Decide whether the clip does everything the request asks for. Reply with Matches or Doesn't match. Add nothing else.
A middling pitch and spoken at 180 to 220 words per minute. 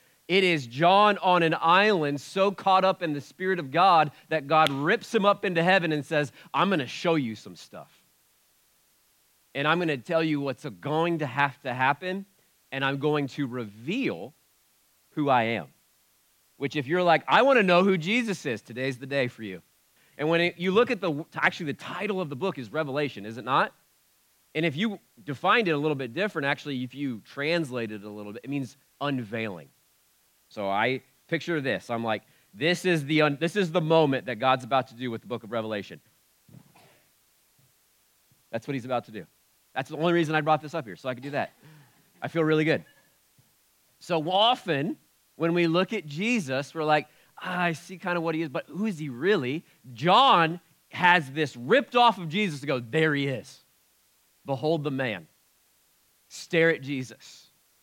Matches